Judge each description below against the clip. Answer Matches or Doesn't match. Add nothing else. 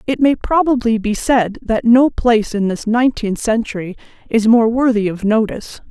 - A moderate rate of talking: Matches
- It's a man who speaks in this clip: Doesn't match